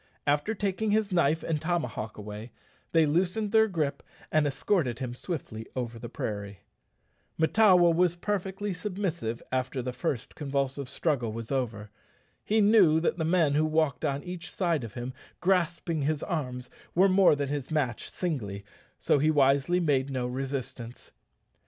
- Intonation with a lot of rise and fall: Yes, wide, 5.8 semitones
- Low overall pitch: No, medium, 150 Hz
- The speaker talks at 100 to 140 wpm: No, average, 155 wpm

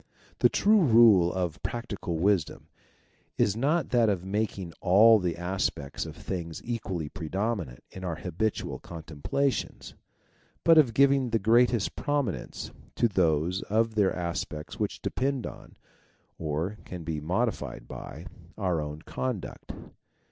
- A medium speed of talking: No, slow, 130 wpm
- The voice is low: Yes, very low, 95 Hz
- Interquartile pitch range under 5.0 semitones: No, wide, 5.5 semitones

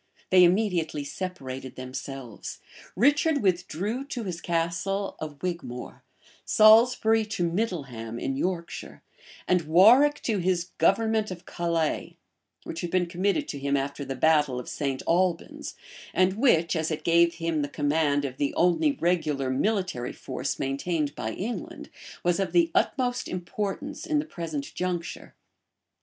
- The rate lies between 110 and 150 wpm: Yes, average, 140 wpm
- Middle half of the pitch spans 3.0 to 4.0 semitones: No, wide, 5.5 semitones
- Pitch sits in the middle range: Yes, medium, 175 Hz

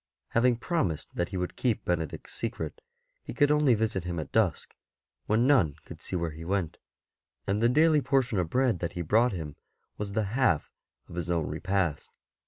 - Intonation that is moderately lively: No, wide, 6.0 semitones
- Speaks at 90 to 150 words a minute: No, average, 190 wpm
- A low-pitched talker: Yes, low, 100 Hz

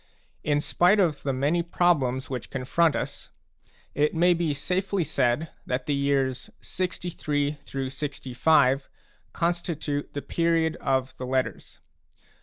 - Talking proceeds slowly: Yes, slow, 120 wpm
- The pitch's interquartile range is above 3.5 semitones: Yes, average, 4.1 semitones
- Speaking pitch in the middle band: Yes, medium, 145 Hz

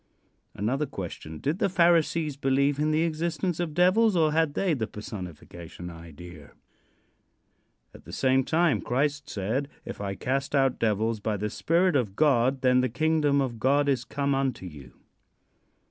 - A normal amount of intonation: No, wide, 6.3 semitones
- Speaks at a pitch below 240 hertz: Yes, low, 135 Hz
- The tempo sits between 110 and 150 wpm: No, average, 160 wpm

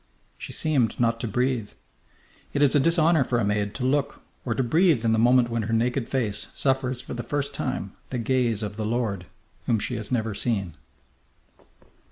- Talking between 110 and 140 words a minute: No, average, 195 wpm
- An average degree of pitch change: Yes, average, 3.1 semitones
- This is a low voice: Yes, low, 120 Hz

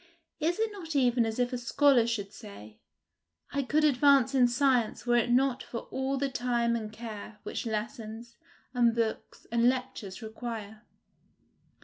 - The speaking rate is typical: Yes, average, 155 wpm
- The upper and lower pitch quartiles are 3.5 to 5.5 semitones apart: No, average, 2.9 semitones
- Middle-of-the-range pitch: No, high, 240 Hz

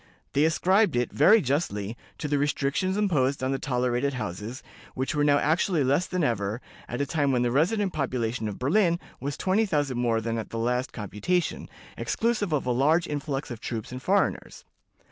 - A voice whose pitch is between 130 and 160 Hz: Yes, medium, 140 Hz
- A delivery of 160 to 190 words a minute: Yes, average, 185 wpm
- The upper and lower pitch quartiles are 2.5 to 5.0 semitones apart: No, wide, 5.4 semitones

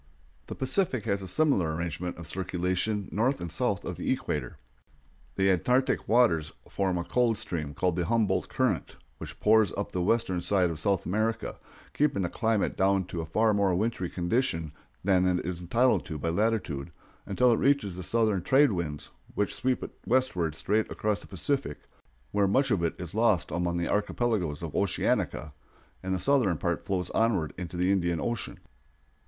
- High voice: No, very low, 95 Hz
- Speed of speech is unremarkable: Yes, average, 180 wpm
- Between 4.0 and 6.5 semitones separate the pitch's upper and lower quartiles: Yes, average, 4.6 semitones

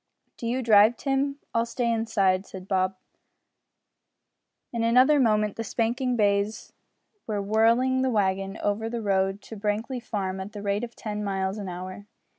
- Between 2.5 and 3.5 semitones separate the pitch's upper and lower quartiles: Yes, average, 3.0 semitones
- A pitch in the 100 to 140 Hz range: No, high, 215 Hz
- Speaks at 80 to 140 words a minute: No, average, 160 wpm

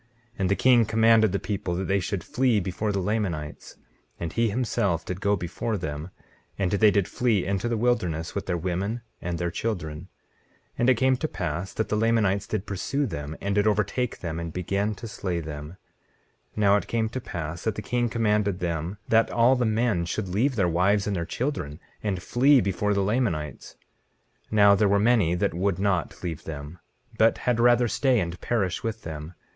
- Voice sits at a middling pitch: No, low, 100 Hz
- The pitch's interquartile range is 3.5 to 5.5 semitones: Yes, average, 4.3 semitones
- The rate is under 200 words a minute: No, fast, 205 wpm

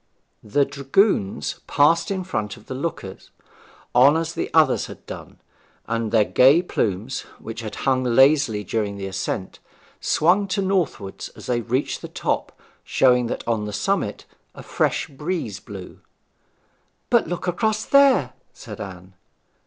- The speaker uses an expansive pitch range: Yes, wide, 8.0 semitones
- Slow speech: No, average, 145 wpm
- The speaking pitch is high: No, low, 130 Hz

